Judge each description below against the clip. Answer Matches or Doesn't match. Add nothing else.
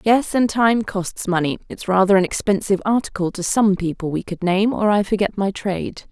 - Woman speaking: Matches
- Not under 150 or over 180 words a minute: Doesn't match